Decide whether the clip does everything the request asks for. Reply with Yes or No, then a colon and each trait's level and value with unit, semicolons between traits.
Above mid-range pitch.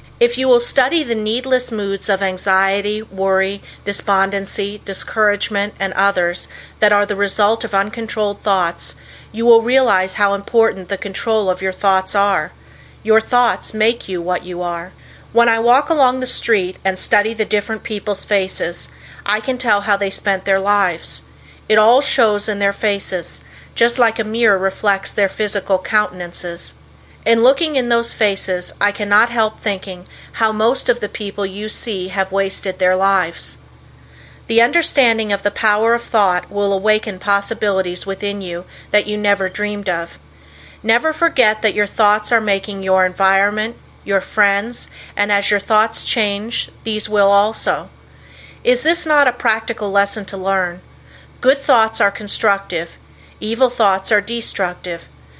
Yes: high, 205 Hz